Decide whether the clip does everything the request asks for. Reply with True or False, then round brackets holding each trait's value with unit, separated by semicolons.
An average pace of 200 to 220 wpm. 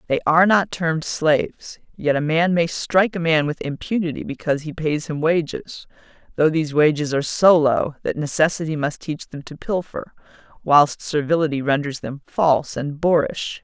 False (170 wpm)